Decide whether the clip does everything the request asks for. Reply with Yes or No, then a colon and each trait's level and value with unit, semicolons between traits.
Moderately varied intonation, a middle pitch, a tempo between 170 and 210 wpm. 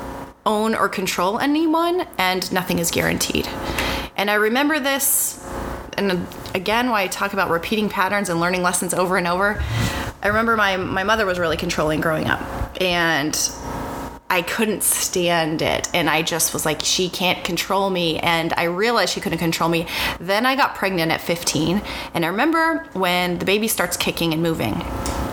Yes: average, 3.6 semitones; medium, 180 Hz; average, 175 wpm